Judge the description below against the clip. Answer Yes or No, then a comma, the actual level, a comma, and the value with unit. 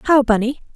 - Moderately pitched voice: No, very high, 250 Hz